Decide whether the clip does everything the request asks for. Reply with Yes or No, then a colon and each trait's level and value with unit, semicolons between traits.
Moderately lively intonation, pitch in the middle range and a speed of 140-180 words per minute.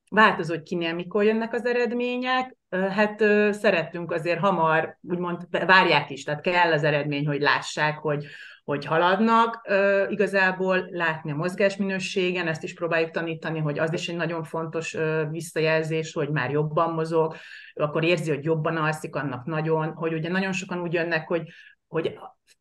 Yes: average, 3.0 semitones; medium, 170 Hz; average, 150 wpm